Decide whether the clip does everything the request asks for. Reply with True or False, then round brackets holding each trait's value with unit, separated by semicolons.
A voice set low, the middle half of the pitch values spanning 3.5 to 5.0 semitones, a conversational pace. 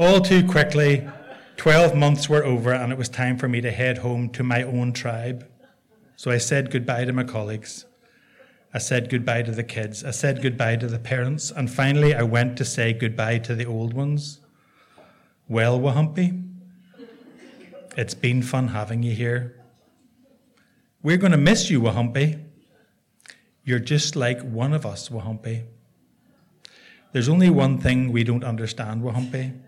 True (130 Hz; 4.1 semitones; 160 wpm)